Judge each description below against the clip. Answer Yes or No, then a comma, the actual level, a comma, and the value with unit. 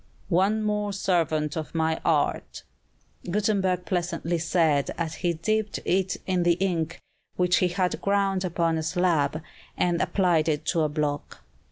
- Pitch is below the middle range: No, medium, 175 Hz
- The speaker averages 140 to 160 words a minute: Yes, average, 150 wpm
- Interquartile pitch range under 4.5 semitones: Yes, average, 2.8 semitones